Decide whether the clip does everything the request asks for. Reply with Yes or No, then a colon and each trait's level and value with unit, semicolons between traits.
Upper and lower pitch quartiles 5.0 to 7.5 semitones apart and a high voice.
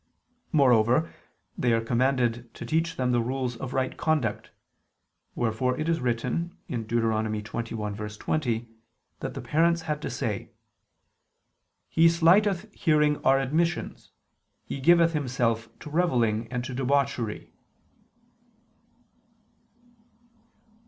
No: wide, 5.4 semitones; low, 130 Hz